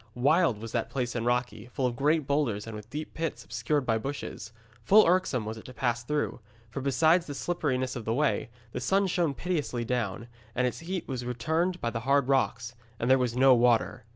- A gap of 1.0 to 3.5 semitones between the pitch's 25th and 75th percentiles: No, average, 4.3 semitones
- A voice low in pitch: Yes, low, 125 Hz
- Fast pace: Yes, fast, 210 wpm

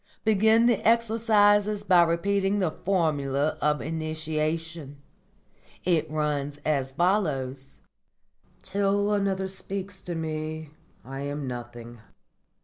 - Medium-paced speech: No, slow, 100 wpm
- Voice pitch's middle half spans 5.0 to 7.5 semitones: Yes, wide, 5.4 semitones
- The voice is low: No, medium, 165 Hz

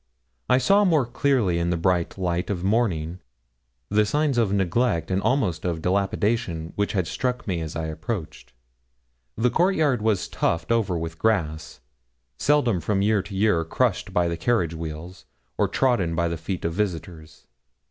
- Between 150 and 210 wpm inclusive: Yes, average, 170 wpm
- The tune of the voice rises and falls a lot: Yes, wide, 5.7 semitones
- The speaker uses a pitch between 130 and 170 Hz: No, very low, 95 Hz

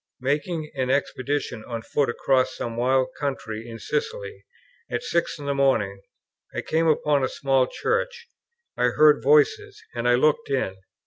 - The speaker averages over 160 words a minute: No, average, 155 wpm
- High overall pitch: No, medium, 140 Hz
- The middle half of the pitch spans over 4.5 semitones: Yes, average, 5.1 semitones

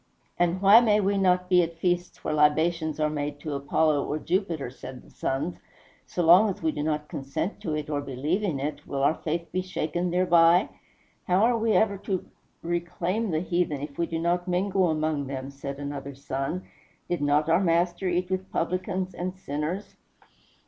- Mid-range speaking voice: Yes, medium, 170 Hz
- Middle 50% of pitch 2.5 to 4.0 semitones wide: Yes, average, 3.6 semitones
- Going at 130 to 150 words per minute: No, average, 190 wpm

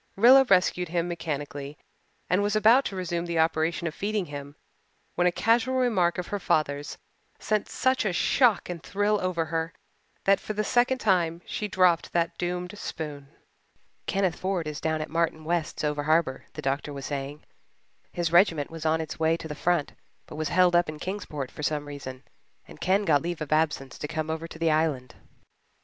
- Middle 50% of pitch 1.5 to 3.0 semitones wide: No, average, 3.4 semitones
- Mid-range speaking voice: Yes, medium, 165 Hz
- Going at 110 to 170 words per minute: No, average, 190 wpm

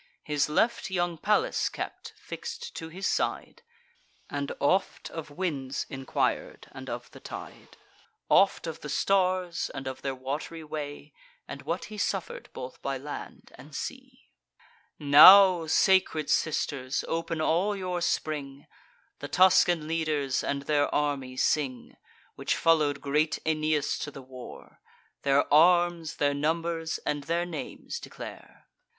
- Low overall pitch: No, medium, 155 Hz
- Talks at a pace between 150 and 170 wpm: No, slow, 135 wpm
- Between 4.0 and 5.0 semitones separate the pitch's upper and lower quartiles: No, average, 3.6 semitones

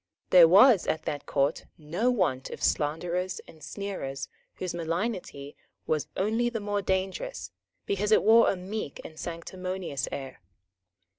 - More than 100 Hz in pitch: Yes, medium, 185 Hz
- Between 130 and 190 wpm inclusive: Yes, average, 140 wpm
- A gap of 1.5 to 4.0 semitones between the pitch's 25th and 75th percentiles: No, average, 4.6 semitones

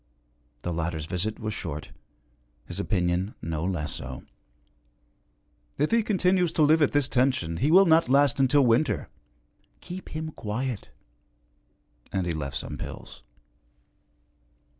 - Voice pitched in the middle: No, low, 120 Hz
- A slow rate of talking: Yes, slow, 130 wpm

